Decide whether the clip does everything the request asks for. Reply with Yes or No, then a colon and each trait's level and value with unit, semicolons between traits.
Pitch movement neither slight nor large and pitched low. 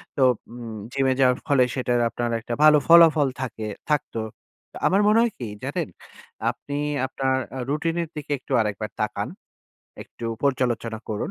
Yes: average, 4.1 semitones; low, 130 Hz